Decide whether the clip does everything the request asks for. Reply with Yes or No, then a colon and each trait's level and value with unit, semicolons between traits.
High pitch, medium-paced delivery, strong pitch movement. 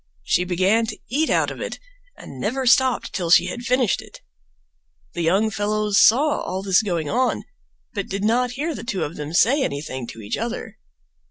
Yes: high, 210 Hz; average, 190 wpm; wide, 5.7 semitones